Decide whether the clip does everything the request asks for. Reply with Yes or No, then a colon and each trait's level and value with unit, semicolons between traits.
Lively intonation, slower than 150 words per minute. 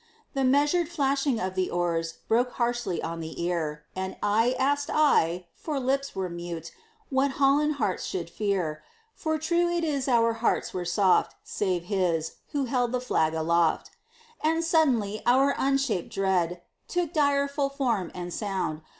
No: wide, 7.9 semitones; average, 155 wpm